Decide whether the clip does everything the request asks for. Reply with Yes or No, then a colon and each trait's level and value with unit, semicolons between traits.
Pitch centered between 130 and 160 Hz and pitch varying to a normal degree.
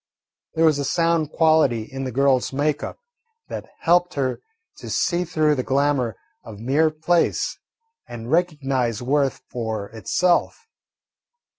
Yes: medium, 140 Hz; average, 4.3 semitones